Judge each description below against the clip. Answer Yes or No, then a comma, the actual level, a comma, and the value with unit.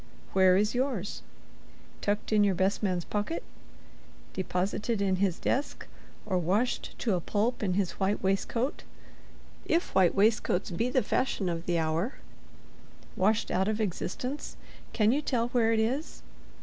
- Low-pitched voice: No, high, 205 Hz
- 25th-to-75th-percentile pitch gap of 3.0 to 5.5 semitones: Yes, average, 3.8 semitones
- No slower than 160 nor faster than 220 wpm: No, average, 140 wpm